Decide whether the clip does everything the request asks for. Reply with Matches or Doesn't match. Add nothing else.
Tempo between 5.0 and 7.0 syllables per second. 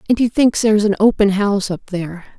Matches